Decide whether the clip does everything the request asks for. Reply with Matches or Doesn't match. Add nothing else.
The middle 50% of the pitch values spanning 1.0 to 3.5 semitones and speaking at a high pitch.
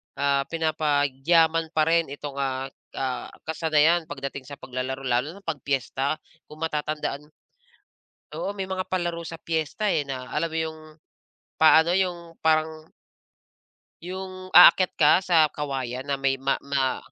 Doesn't match